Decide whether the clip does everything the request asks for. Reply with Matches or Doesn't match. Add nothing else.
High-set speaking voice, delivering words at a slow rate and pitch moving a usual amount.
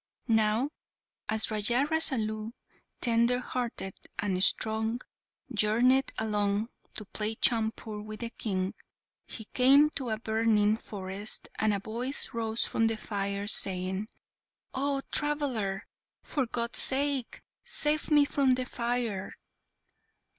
Matches